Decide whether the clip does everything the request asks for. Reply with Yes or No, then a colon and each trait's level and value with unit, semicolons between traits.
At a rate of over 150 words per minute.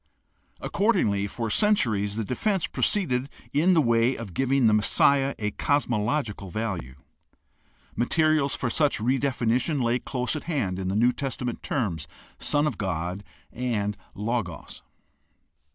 No: slow, 135 wpm